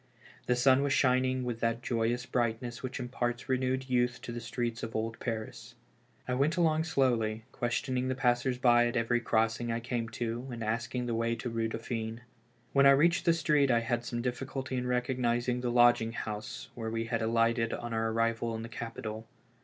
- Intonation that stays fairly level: Yes, narrow, 1.8 semitones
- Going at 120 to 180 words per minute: No, average, 195 wpm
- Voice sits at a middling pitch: No, low, 120 Hz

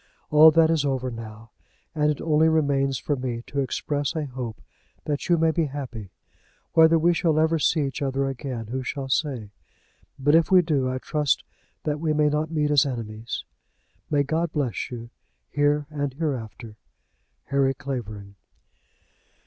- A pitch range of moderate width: Yes, average, 3.2 semitones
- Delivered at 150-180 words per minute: Yes, average, 165 wpm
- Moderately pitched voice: Yes, medium, 145 Hz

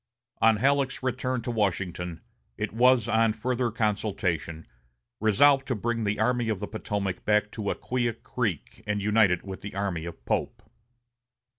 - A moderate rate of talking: Yes, average, 155 wpm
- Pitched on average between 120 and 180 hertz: No, low, 110 Hz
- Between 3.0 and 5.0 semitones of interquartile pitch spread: Yes, average, 3.4 semitones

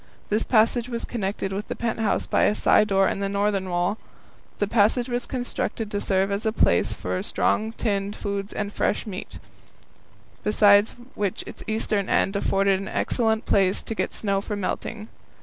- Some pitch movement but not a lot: No, narrow, 2.0 semitones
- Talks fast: No, average, 180 wpm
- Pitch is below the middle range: No, high, 205 Hz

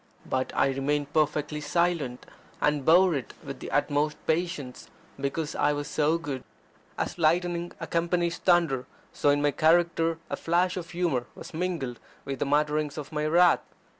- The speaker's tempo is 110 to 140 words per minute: No, average, 160 wpm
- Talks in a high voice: No, medium, 155 Hz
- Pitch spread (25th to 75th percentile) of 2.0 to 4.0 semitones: Yes, average, 2.9 semitones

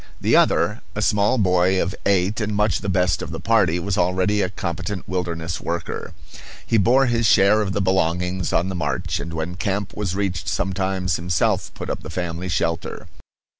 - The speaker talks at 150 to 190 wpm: Yes, average, 185 wpm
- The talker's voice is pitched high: No, very low, 95 Hz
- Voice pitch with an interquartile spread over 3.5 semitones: No, narrow, 2.5 semitones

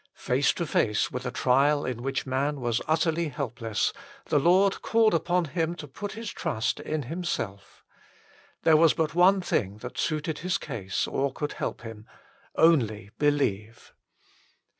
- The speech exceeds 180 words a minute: No, average, 160 wpm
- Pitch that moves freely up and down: Yes, wide, 5.9 semitones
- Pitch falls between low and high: Yes, medium, 145 Hz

